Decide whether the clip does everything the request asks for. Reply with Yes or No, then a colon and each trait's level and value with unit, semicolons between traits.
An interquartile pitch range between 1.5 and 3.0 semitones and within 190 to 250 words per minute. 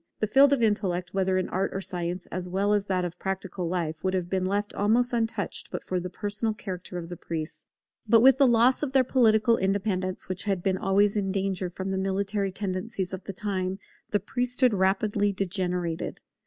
Yes: narrow, 2.4 semitones; average, 200 wpm